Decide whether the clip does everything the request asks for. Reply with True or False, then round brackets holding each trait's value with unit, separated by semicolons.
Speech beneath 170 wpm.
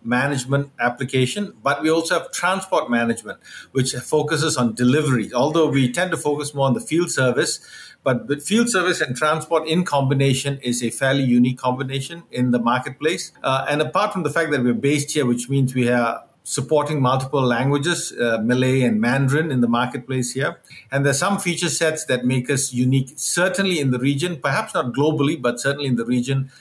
False (190 wpm)